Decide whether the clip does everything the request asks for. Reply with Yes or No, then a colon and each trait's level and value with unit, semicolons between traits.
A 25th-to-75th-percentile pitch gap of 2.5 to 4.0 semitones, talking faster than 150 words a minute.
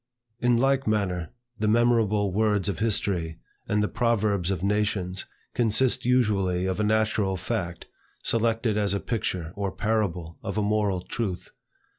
No: average, 3.0 semitones; average, 145 wpm